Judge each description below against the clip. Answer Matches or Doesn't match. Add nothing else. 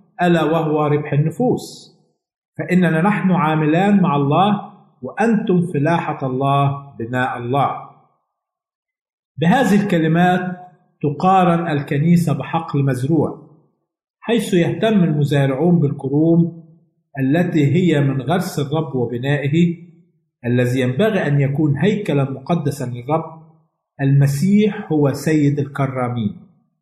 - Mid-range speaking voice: Matches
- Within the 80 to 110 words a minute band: Matches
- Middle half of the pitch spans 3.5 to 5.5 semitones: Matches